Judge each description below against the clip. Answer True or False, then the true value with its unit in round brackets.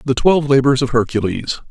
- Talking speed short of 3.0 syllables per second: False (6.0 syllables/s)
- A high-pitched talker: False (130 Hz)